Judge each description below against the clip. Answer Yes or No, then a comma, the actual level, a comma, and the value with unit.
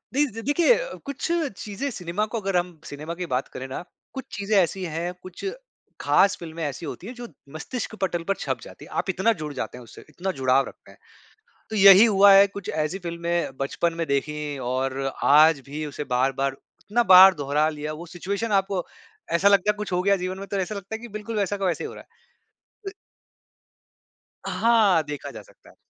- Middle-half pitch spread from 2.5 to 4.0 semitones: No, average, 5.0 semitones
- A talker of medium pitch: Yes, medium, 180 Hz